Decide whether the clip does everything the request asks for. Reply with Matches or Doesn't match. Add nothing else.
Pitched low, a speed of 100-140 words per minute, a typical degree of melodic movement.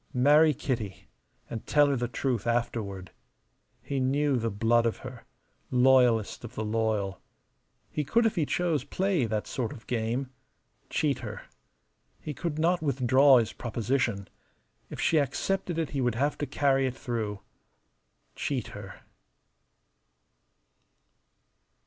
Matches